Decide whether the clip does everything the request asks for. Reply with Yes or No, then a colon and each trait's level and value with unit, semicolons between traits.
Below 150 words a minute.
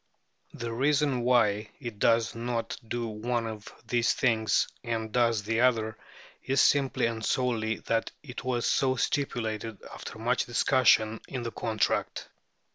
Yes: average, 140 wpm